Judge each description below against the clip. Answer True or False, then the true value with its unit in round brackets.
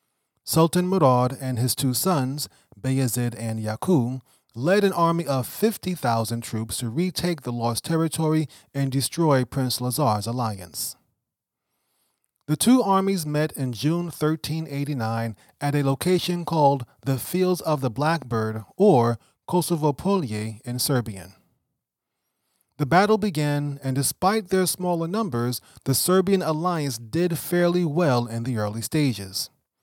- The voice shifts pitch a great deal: True (6.2 semitones)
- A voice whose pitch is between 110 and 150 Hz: True (140 Hz)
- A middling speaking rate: False (130 wpm)